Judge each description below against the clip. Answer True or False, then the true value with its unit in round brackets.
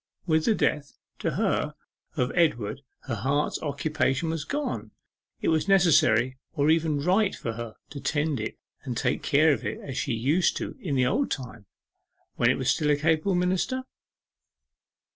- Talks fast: False (170 wpm)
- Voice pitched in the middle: True (150 Hz)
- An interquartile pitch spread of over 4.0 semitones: True (4.4 semitones)